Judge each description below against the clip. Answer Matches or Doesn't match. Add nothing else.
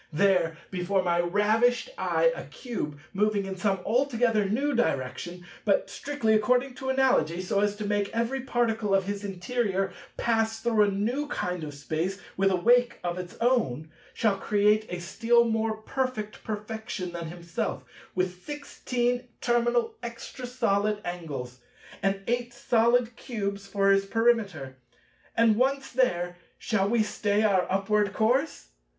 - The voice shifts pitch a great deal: Doesn't match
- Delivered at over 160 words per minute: Doesn't match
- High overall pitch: Matches